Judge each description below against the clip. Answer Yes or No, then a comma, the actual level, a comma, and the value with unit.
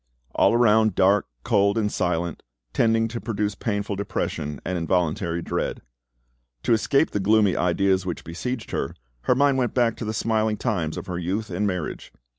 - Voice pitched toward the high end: No, low, 105 Hz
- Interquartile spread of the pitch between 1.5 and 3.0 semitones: No, average, 3.8 semitones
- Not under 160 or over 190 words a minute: Yes, average, 170 wpm